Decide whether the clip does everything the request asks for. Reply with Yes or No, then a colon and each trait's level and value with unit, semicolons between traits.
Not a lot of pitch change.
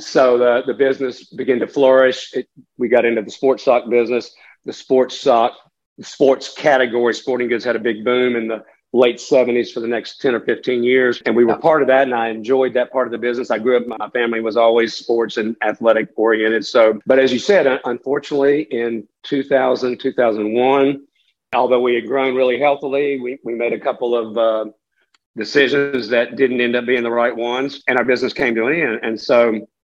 Yes: narrow, 2.1 semitones